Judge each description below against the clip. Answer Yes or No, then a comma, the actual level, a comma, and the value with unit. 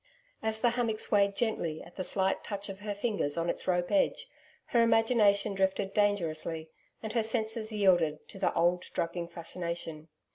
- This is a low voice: No, high, 200 Hz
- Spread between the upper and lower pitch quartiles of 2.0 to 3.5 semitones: No, average, 4.2 semitones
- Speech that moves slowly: No, average, 170 wpm